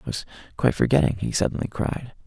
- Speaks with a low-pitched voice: Yes, low, 110 Hz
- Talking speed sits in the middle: Yes, average, 185 wpm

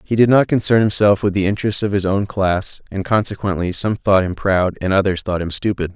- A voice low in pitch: Yes, low, 100 Hz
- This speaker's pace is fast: Yes, fast, 230 wpm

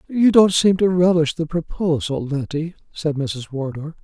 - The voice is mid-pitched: Yes, medium, 160 Hz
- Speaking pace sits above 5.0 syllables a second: No, 4.5 syllables/s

